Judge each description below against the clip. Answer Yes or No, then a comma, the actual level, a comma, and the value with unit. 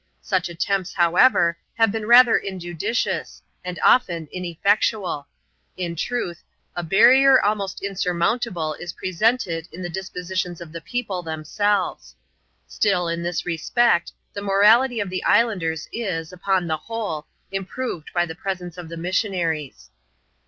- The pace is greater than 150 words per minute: No, slow, 135 wpm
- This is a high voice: No, medium, 180 Hz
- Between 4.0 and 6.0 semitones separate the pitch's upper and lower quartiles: No, average, 3.5 semitones